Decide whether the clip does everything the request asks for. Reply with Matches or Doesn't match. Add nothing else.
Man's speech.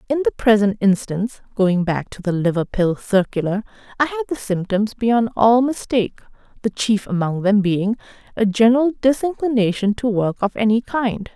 Doesn't match